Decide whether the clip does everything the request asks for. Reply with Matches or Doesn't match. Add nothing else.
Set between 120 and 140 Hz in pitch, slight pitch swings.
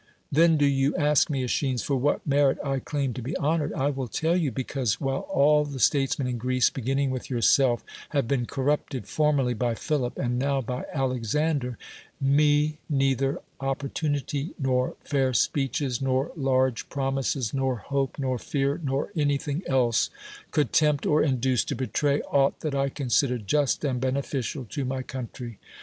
Matches